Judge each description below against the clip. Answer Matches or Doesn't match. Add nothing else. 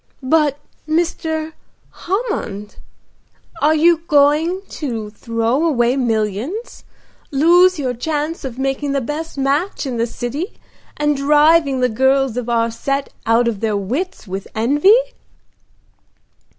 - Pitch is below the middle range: Doesn't match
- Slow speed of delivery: Matches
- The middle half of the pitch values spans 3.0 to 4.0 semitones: Doesn't match